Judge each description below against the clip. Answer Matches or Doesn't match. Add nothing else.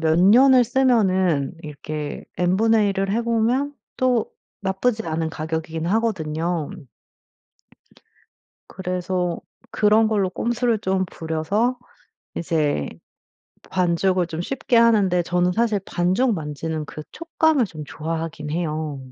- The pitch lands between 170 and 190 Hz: Matches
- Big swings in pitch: Matches